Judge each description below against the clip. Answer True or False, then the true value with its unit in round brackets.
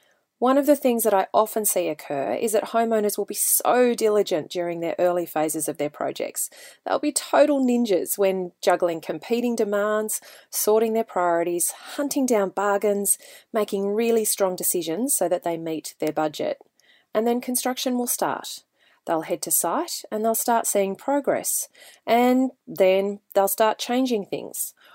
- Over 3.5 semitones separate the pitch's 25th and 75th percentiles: True (5.2 semitones)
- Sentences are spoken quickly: False (160 wpm)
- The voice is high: True (210 Hz)